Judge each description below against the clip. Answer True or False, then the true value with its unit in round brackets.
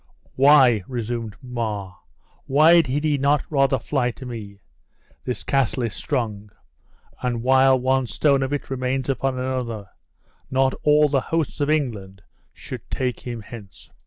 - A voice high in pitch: False (130 Hz)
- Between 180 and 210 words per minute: False (145 wpm)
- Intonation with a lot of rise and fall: False (2.8 semitones)